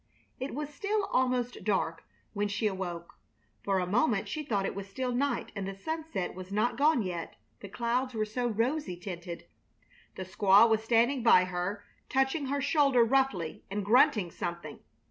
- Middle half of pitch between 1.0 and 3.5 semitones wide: No, wide, 5.5 semitones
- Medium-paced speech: Yes, average, 170 wpm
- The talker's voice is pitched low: No, high, 220 Hz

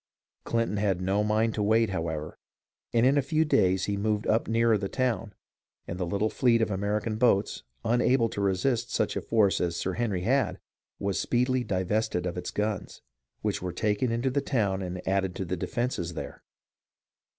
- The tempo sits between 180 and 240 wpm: Yes, average, 185 wpm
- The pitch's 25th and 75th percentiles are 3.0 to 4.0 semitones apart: Yes, average, 3.6 semitones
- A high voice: No, low, 105 Hz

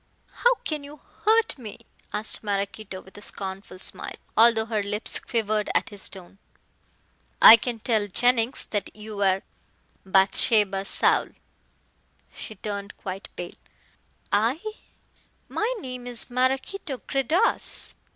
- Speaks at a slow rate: Yes, slow, 120 wpm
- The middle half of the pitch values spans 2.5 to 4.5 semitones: Yes, average, 4.0 semitones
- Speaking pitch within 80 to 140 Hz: No, high, 215 Hz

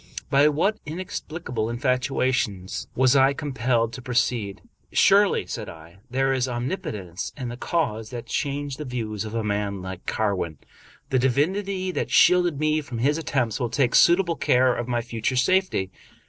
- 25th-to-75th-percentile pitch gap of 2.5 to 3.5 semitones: No, average, 4.7 semitones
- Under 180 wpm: Yes, average, 170 wpm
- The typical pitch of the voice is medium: No, low, 130 Hz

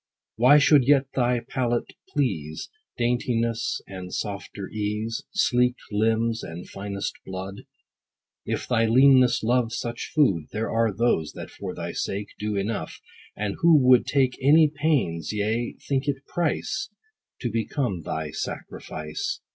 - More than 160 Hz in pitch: No, low, 115 Hz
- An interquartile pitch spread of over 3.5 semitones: Yes, average, 4.4 semitones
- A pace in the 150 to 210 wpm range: No, slow, 135 wpm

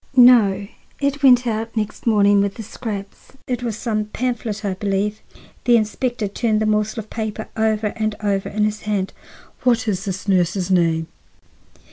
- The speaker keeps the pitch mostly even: Yes, narrow, 2.3 semitones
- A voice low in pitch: No, high, 215 Hz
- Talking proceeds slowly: No, average, 165 wpm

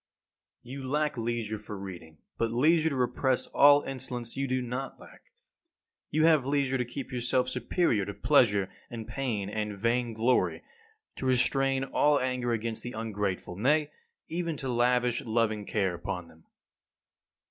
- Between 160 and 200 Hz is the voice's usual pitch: No, low, 125 Hz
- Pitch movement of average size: Yes, average, 3.8 semitones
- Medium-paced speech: Yes, average, 155 wpm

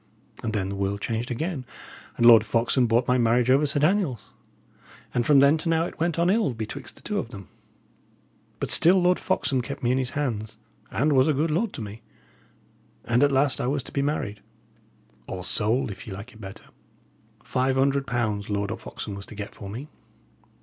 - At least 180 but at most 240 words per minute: Yes, fast, 205 wpm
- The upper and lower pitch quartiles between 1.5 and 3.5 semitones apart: No, average, 4.9 semitones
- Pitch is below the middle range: Yes, low, 125 Hz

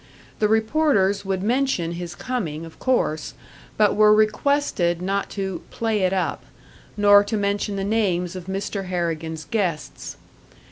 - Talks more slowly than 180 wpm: Yes, average, 140 wpm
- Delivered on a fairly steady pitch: No, average, 3.5 semitones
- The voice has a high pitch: Yes, high, 200 Hz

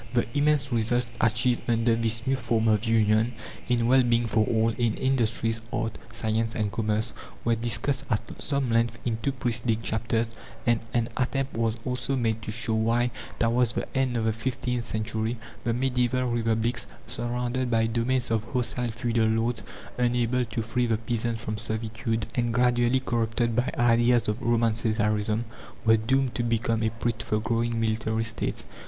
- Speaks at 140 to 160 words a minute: No, average, 170 wpm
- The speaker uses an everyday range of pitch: No, narrow, 1.5 semitones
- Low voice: Yes, low, 115 Hz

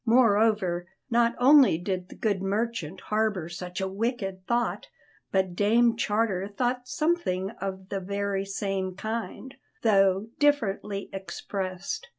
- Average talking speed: No, slow, 125 wpm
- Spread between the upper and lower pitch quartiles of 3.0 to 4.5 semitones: Yes, average, 3.5 semitones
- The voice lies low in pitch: No, high, 200 Hz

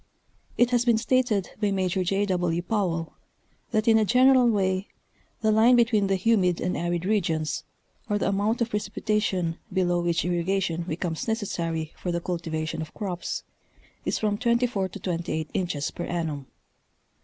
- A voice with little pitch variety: No, average, 4.1 semitones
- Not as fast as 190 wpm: Yes, average, 155 wpm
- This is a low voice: No, high, 190 Hz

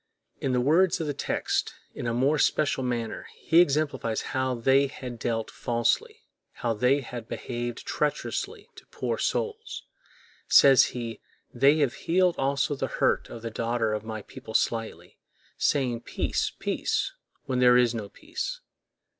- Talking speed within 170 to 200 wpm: No, average, 155 wpm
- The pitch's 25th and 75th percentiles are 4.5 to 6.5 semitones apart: No, average, 3.5 semitones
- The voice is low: Yes, low, 125 Hz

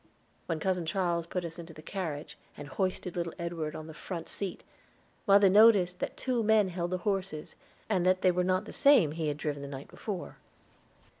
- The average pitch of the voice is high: No, medium, 180 Hz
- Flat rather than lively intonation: No, average, 3.2 semitones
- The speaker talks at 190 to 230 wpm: Yes, average, 200 wpm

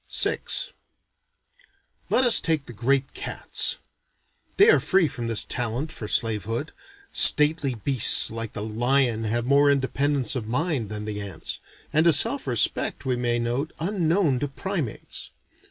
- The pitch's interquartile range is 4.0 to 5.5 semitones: Yes, average, 4.6 semitones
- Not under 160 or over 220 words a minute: No, average, 150 wpm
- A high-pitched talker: No, low, 130 Hz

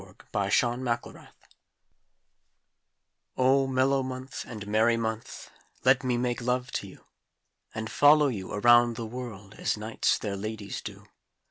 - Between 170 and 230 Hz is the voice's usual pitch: No, low, 120 Hz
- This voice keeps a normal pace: No, slow, 130 wpm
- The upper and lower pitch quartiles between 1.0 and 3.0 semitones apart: Yes, average, 2.7 semitones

